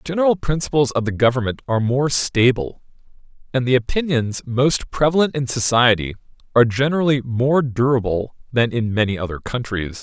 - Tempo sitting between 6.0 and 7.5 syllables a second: No, 5.6 syllables/s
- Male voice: Yes, male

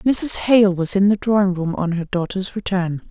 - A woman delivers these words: Yes, female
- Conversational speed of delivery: No, fast, 215 wpm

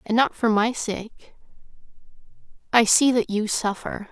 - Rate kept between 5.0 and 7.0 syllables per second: No, 4.2 syllables/s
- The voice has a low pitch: No, high, 225 Hz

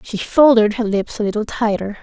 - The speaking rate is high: Yes, fast, 210 wpm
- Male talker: No, female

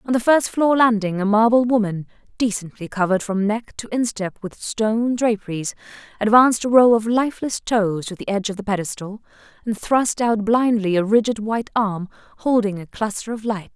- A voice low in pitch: No, high, 215 Hz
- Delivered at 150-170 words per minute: No, average, 185 wpm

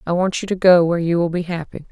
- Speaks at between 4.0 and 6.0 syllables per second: No, 6.8 syllables/s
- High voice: No, medium, 175 Hz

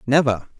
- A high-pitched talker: No, low, 130 Hz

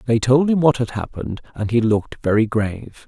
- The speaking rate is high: Yes, fast, 215 wpm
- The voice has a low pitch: Yes, low, 120 Hz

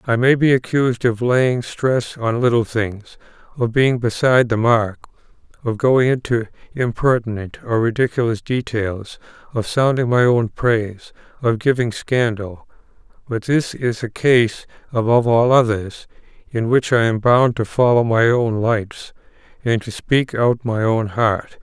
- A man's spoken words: Yes, male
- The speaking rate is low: No, average, 155 wpm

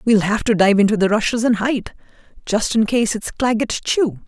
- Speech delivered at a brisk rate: Yes, fast, 210 wpm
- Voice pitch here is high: Yes, high, 220 Hz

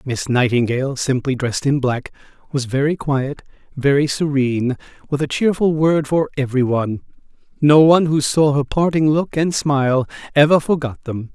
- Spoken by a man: Yes, male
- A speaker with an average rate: Yes, average, 155 wpm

